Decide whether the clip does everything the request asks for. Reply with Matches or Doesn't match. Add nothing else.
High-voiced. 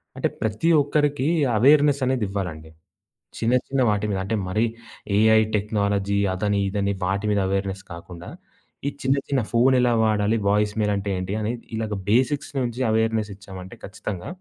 Doesn't match